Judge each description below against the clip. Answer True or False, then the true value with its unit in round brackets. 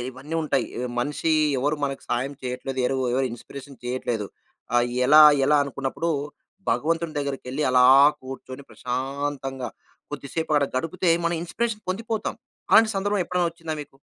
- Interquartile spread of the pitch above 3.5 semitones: True (4.1 semitones)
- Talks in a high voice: False (140 Hz)